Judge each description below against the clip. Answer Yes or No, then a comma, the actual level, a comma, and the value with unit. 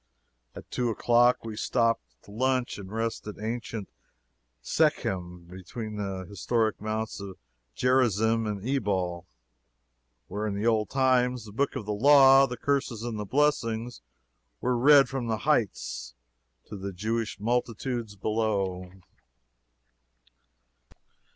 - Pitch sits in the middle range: No, low, 110 Hz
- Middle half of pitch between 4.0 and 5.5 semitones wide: No, average, 3.4 semitones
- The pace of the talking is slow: Yes, slow, 125 wpm